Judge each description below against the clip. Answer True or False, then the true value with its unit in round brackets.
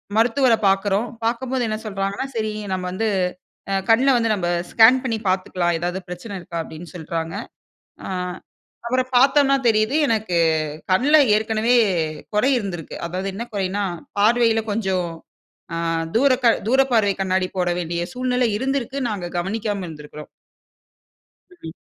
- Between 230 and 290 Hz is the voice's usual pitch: False (215 Hz)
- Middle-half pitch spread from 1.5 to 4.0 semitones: False (4.8 semitones)